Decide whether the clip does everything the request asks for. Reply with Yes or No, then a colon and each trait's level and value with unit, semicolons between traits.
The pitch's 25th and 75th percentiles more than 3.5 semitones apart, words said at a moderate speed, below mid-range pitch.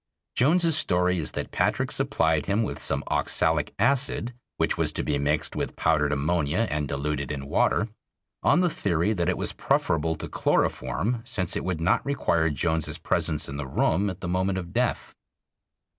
Yes: average, 5.3 semitones; average, 175 wpm; very low, 85 Hz